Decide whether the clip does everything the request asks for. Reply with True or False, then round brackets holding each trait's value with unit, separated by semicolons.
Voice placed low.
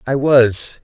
True (130 Hz)